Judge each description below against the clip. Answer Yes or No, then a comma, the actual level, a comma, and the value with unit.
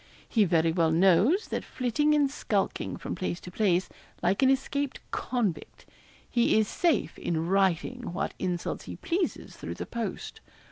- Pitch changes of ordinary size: No, wide, 7.0 semitones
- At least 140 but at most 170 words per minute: Yes, average, 155 wpm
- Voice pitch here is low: No, high, 205 Hz